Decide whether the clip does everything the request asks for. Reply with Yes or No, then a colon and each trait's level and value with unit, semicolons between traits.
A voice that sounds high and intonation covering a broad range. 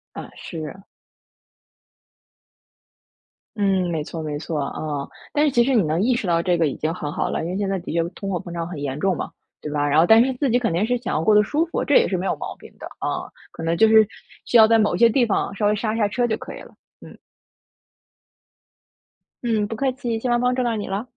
Yes: high, 205 Hz; wide, 5.9 semitones